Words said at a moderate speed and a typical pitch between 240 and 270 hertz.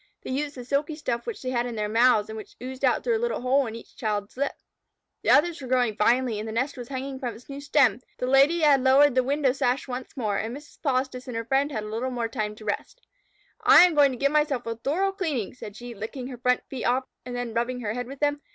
No: fast, 260 wpm; very high, 255 Hz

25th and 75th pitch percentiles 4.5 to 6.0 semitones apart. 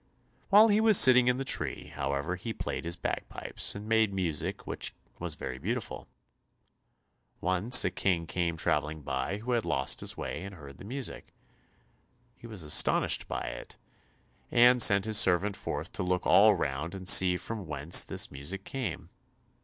Yes: wide, 5.6 semitones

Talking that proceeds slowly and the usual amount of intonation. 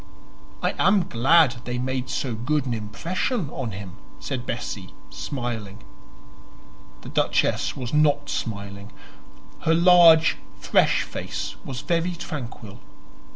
No: slow, 115 wpm; wide, 6.2 semitones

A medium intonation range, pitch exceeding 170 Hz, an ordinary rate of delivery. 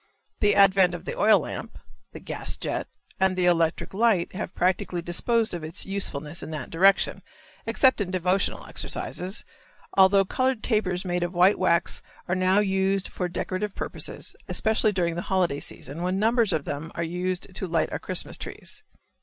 No: narrow, 2.3 semitones; medium, 185 Hz; average, 170 wpm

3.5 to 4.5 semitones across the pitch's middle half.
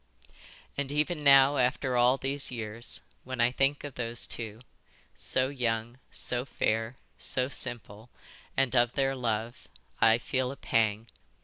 No: average, 2.8 semitones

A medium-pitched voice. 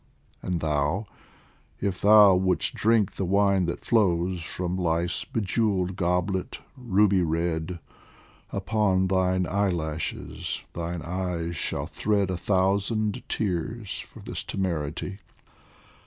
No: very low, 95 Hz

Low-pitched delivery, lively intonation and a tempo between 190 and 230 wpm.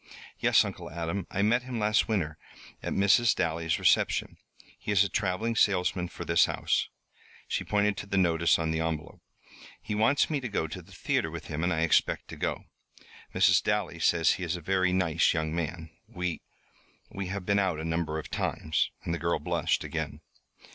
No: very low, 90 Hz; average, 3.6 semitones; average, 195 wpm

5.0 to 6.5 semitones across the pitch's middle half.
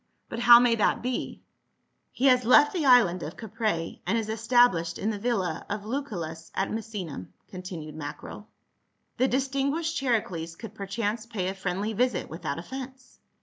Yes: wide, 5.4 semitones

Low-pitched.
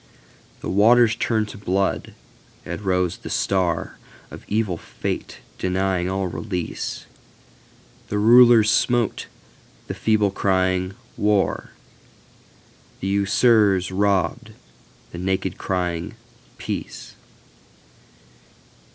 Yes: very low, 95 Hz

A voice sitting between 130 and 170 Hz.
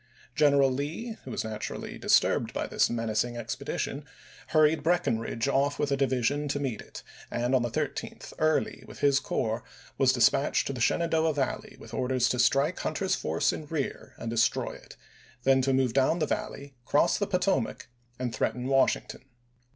Yes: low, 135 Hz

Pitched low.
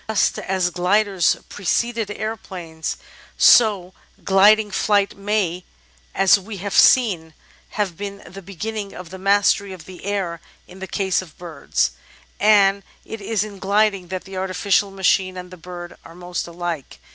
No: high, 195 Hz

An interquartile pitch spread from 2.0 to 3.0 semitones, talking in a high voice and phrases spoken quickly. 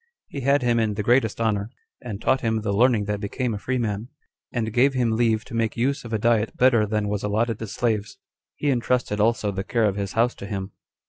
No: average, 2.7 semitones; low, 115 Hz; fast, 235 wpm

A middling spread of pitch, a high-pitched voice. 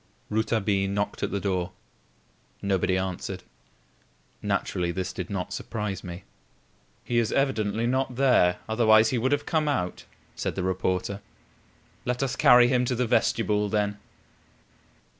No: average, 4.5 semitones; low, 105 Hz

